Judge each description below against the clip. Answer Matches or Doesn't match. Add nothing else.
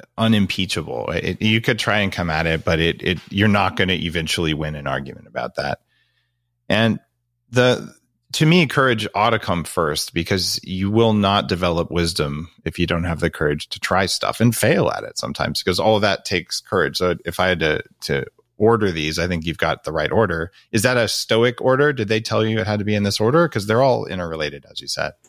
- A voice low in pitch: Matches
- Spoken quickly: Matches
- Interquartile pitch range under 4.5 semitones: Doesn't match